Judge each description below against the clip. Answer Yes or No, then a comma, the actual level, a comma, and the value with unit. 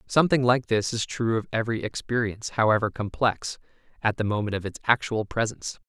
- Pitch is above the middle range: No, low, 115 Hz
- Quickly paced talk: No, average, 175 wpm